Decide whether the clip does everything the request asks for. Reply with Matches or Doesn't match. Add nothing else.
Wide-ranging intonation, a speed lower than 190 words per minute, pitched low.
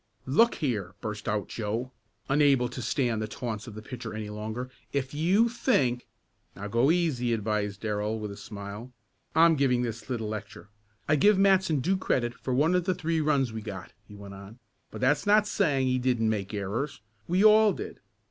Doesn't match